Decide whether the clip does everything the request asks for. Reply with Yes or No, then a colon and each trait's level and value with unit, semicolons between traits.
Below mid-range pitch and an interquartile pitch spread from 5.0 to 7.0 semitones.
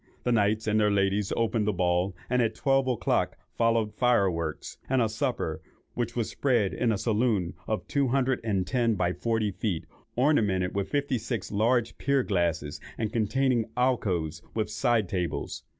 No: low, 110 Hz; average, 3.8 semitones